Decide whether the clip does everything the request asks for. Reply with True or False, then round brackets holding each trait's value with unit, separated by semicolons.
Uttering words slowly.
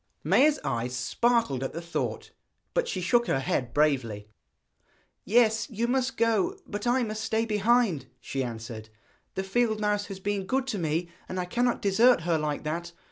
False (175 wpm)